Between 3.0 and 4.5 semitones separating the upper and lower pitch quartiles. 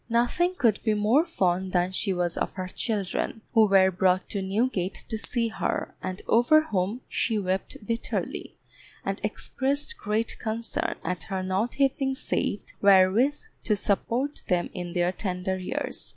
Yes: average, 4.2 semitones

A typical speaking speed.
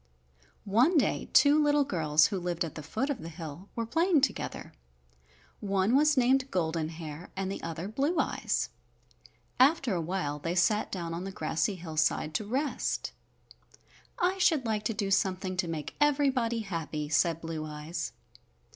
Yes: average, 165 wpm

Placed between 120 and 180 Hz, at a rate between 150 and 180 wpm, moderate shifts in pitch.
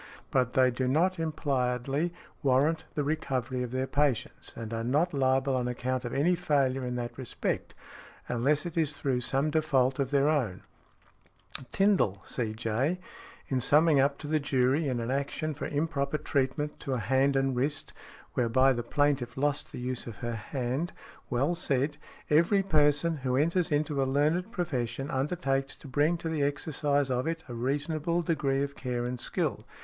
Yes: medium, 140 Hz; average, 170 wpm; average, 3.2 semitones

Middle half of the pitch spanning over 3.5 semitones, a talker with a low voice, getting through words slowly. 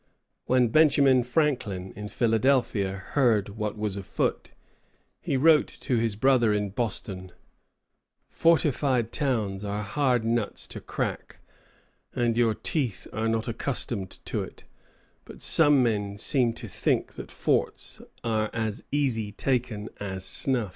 Yes: average, 4.0 semitones; low, 115 Hz; slow, 125 wpm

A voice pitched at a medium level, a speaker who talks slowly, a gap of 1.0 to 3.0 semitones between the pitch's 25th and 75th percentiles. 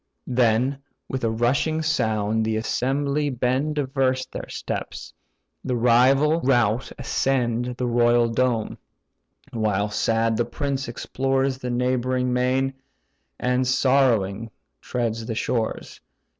No: low, 125 Hz; slow, 115 wpm; narrow, 2.6 semitones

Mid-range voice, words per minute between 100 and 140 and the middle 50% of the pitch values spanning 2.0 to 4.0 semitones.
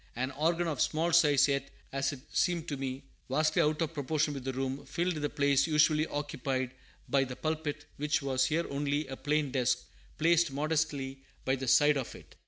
No: medium, 145 Hz; average, 190 wpm; narrow, 2.5 semitones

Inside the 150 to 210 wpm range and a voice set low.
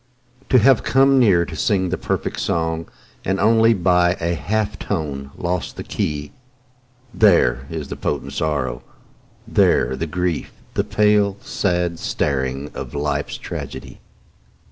No: slow, 135 wpm; very low, 85 Hz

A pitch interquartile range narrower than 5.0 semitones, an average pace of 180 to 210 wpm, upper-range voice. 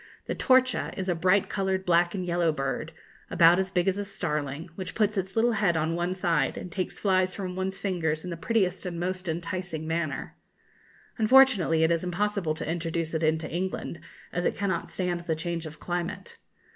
No: narrow, 2.5 semitones; average, 195 wpm; medium, 175 Hz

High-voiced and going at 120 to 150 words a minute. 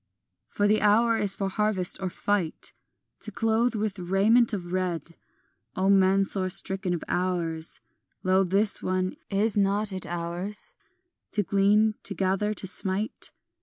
Yes: high, 195 Hz; average, 145 wpm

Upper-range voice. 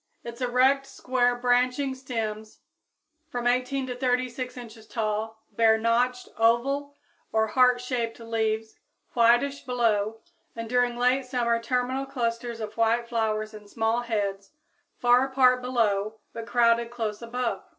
Yes: high, 240 Hz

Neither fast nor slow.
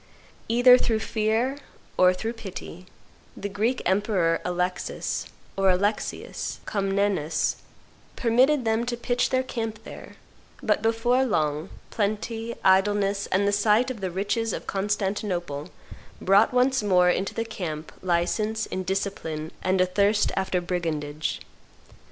No: slow, 125 wpm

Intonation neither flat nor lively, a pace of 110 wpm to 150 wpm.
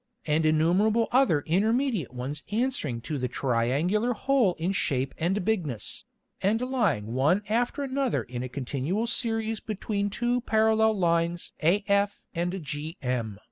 No: wide, 7.2 semitones; slow, 135 wpm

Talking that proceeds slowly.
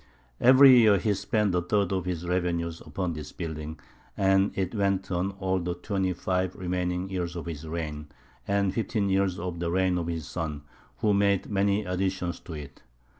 No: average, 180 wpm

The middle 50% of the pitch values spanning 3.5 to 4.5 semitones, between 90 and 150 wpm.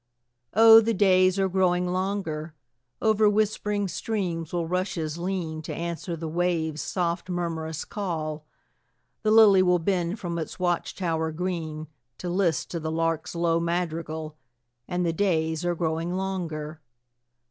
No: narrow, 2.6 semitones; average, 140 wpm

